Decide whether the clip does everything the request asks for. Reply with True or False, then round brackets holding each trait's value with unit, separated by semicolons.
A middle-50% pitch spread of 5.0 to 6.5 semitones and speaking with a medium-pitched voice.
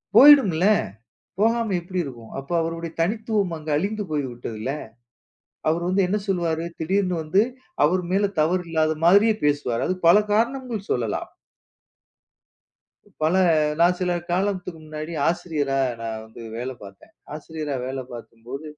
True (5.4 semitones; 165 Hz)